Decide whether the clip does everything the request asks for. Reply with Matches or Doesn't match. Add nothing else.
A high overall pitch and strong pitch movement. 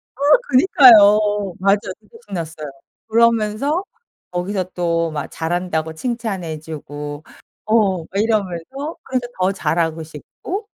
Matches